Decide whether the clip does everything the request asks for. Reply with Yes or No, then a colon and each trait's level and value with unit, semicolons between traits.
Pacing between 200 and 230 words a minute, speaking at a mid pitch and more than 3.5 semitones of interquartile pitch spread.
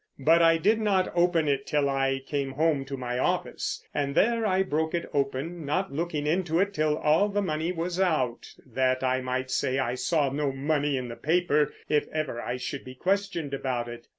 Yes: fast, 205 wpm; medium, 150 Hz; average, 4.2 semitones